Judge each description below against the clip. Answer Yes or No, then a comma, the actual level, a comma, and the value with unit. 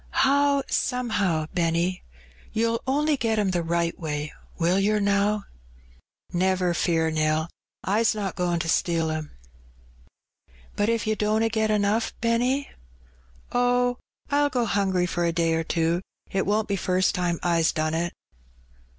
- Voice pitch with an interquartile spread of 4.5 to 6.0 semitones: Yes, average, 5.0 semitones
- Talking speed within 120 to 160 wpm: Yes, average, 145 wpm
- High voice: Yes, high, 195 Hz